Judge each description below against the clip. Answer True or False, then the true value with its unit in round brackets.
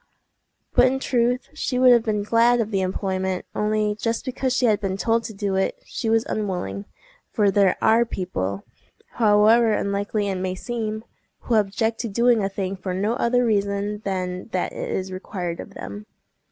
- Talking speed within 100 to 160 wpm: False (175 wpm)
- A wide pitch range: False (3.2 semitones)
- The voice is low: False (210 Hz)